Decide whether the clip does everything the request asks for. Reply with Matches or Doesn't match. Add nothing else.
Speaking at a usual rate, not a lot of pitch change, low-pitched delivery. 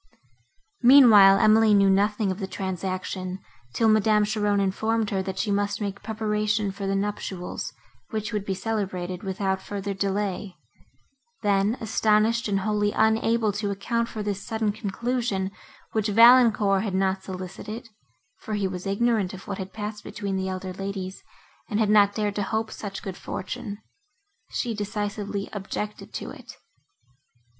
Doesn't match